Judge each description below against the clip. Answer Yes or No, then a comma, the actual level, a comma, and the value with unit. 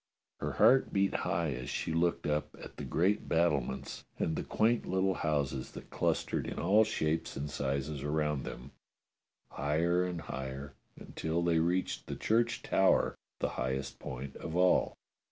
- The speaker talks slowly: No, average, 155 wpm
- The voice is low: Yes, very low, 80 Hz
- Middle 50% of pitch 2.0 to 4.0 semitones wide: No, average, 4.5 semitones